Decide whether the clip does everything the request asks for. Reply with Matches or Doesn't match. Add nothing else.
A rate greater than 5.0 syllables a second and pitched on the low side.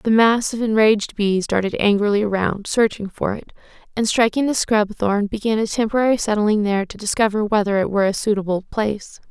Doesn't match